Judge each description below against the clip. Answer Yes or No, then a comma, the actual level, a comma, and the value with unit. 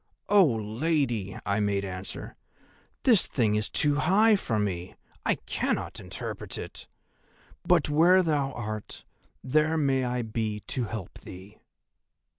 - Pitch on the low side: Yes, low, 120 Hz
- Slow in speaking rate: Yes, slow, 130 wpm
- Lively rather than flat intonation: Yes, wide, 6.5 semitones